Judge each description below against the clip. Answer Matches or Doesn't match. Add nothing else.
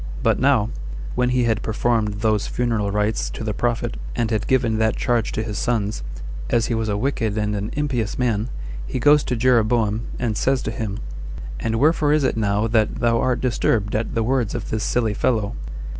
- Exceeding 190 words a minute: Matches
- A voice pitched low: Matches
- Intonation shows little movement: Matches